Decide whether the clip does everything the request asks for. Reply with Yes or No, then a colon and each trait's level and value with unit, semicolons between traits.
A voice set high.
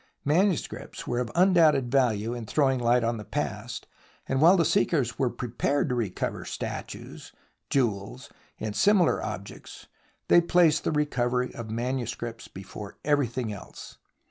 No: low, 125 Hz